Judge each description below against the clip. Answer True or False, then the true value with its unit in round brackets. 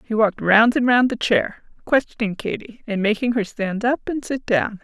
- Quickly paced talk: True (210 wpm)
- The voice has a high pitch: True (225 Hz)